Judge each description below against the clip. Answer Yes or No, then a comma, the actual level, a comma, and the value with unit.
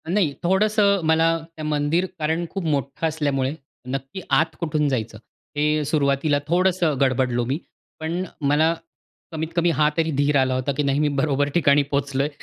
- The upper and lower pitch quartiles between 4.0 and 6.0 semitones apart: No, average, 2.8 semitones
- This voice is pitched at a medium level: Yes, medium, 150 Hz